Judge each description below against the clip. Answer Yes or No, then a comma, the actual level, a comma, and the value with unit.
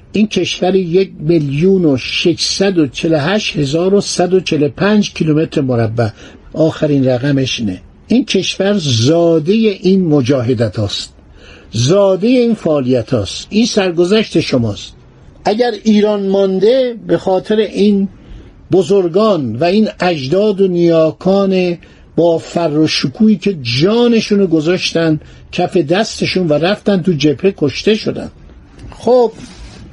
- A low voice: No, medium, 180 Hz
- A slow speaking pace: Yes, slow, 95 wpm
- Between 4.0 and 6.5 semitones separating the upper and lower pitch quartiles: Yes, average, 5.1 semitones